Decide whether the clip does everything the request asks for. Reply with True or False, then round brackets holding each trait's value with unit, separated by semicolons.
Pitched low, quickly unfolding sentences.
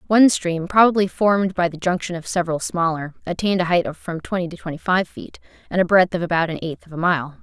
False (175 Hz; 240 wpm)